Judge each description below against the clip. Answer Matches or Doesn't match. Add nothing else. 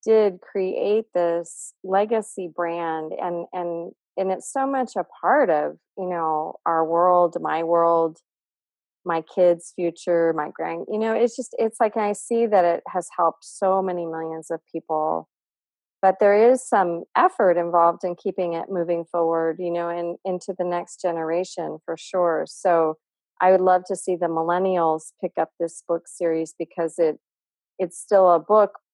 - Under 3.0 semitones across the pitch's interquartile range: Matches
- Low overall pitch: Doesn't match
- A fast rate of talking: Doesn't match